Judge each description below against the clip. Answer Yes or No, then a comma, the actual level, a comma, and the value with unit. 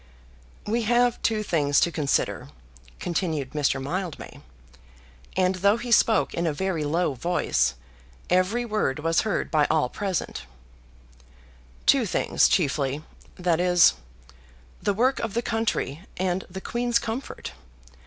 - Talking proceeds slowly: Yes, slow, 130 wpm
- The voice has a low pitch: No, medium, 180 Hz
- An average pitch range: No, wide, 6.0 semitones